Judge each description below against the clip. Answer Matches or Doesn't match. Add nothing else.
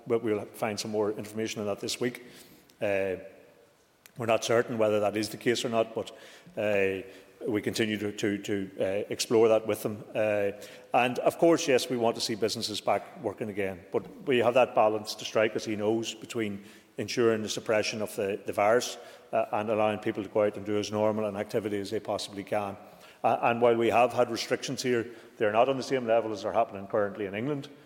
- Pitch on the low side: Matches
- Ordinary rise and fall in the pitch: Doesn't match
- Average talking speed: Doesn't match